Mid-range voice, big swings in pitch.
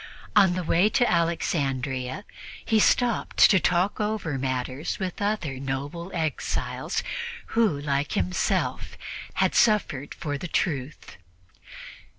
Yes: medium, 165 Hz; wide, 6.3 semitones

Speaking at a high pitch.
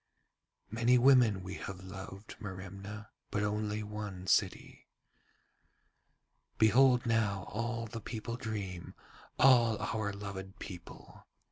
No: low, 105 Hz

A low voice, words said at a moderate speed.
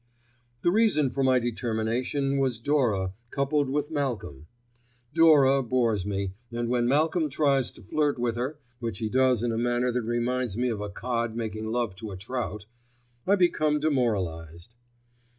Yes: low, 120 Hz; average, 160 wpm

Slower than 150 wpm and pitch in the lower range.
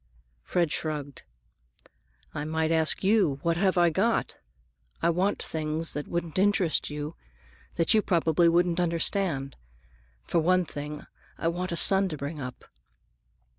No: average, 140 wpm; medium, 165 Hz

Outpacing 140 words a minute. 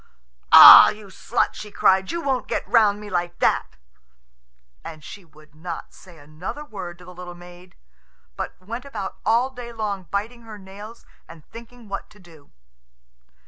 Yes: average, 165 wpm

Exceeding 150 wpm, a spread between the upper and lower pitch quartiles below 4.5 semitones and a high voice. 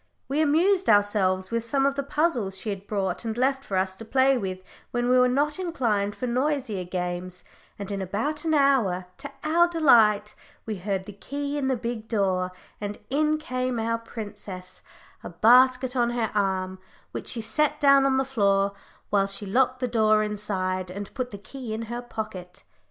No: average, 190 wpm; average, 5.3 semitones; high, 225 Hz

